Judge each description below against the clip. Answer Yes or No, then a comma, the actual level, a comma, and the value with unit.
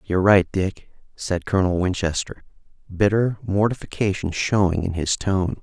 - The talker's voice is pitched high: No, very low, 95 Hz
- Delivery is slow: Yes, slow, 130 wpm